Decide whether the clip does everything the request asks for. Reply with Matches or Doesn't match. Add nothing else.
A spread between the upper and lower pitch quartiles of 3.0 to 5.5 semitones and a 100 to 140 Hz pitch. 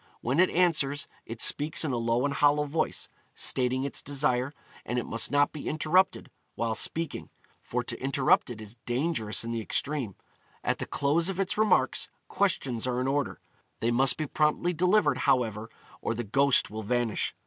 Matches